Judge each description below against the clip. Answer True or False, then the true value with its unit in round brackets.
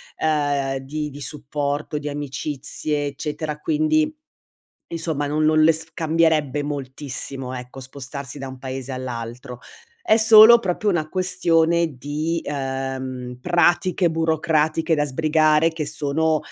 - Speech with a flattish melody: False (3.1 semitones)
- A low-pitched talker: False (150 Hz)